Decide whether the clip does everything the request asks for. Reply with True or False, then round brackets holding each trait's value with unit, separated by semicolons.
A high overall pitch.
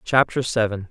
False (110 Hz)